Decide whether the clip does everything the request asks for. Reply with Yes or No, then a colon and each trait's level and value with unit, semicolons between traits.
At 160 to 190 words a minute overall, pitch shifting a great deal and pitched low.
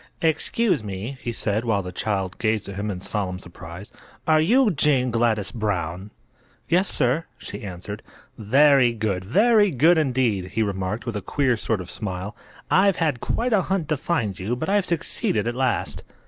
Yes: average, 175 wpm; wide, 7.3 semitones; low, 115 Hz